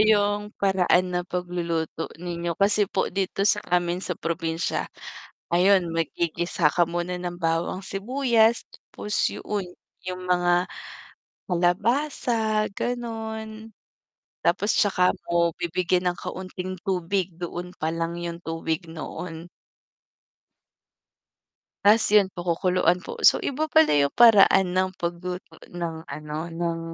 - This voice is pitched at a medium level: Yes, medium, 180 Hz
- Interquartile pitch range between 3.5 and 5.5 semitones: No, average, 3.0 semitones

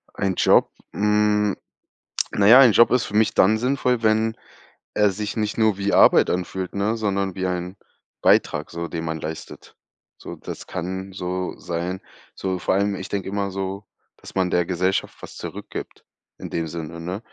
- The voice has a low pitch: Yes, very low, 95 Hz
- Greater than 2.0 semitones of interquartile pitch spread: Yes, narrow, 2.6 semitones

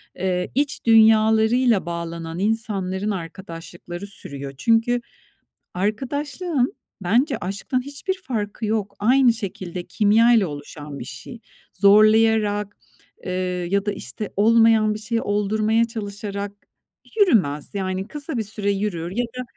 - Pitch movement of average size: Yes, average, 3.4 semitones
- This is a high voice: Yes, high, 210 Hz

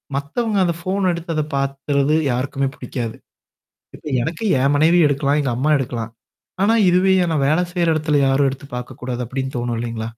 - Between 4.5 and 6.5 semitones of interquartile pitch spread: No, average, 4.1 semitones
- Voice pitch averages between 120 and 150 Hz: Yes, medium, 140 Hz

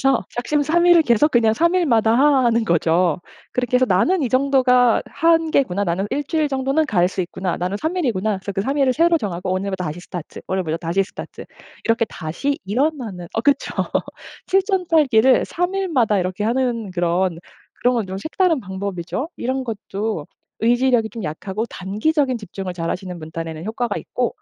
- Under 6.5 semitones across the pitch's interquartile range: No, wide, 6.8 semitones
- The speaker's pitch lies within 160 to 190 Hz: No, high, 230 Hz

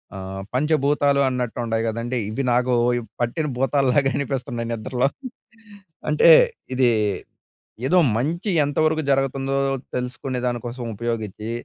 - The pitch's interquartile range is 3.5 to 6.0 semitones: No, average, 3.0 semitones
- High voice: No, low, 130 Hz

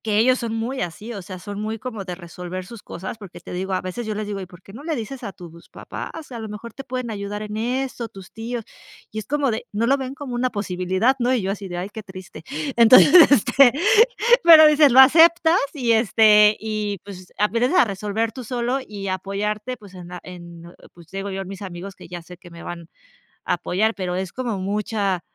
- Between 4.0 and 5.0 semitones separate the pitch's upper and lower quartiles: Yes, average, 4.3 semitones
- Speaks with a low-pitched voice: No, high, 210 Hz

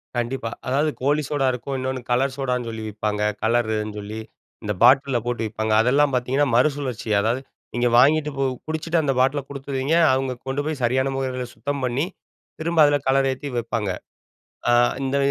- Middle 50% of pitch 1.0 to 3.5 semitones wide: Yes, average, 2.8 semitones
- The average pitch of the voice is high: No, low, 130 Hz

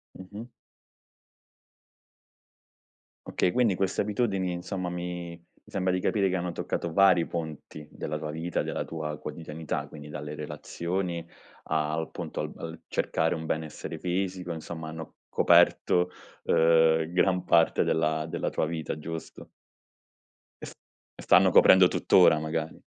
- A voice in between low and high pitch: No, very low, 85 Hz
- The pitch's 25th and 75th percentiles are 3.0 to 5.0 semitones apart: No, narrow, 2.4 semitones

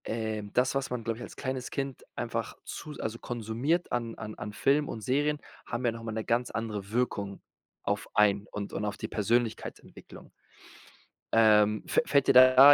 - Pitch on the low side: Yes, low, 115 Hz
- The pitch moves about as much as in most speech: Yes, average, 3.2 semitones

